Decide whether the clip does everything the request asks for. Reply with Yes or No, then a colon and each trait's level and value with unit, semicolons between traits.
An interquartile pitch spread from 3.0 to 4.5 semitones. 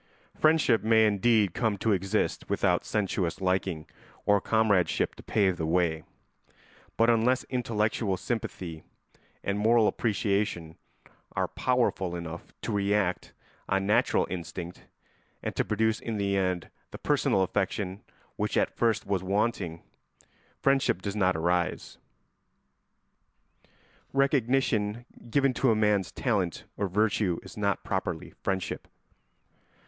Yes: average, 3.4 semitones